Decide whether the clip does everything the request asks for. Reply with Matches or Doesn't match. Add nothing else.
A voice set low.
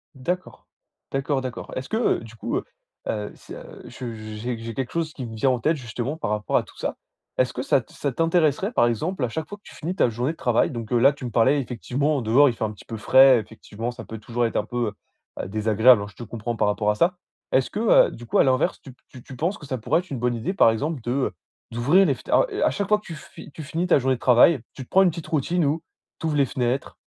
Matches